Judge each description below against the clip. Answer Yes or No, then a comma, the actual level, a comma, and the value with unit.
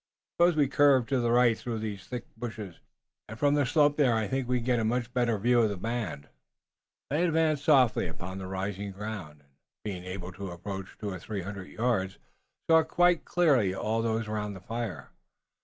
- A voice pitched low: Yes, low, 110 Hz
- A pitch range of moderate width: Yes, average, 4.7 semitones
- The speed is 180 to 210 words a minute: Yes, average, 195 wpm